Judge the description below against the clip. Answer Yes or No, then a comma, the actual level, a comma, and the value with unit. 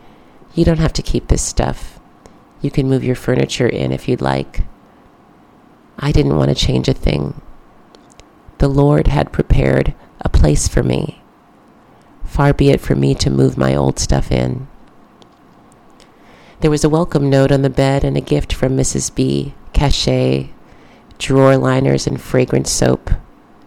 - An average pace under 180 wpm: Yes, average, 155 wpm